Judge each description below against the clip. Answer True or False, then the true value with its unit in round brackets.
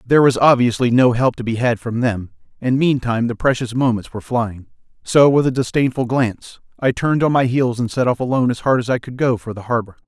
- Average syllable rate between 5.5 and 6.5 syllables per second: True (6.0 syllables/s)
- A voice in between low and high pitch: False (125 Hz)